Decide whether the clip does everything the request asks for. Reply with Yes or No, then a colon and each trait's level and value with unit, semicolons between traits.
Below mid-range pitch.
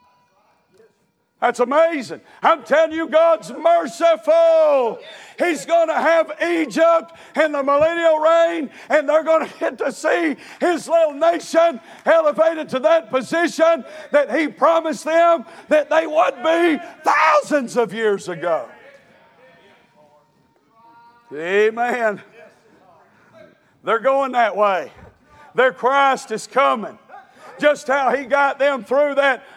No: very high, 295 Hz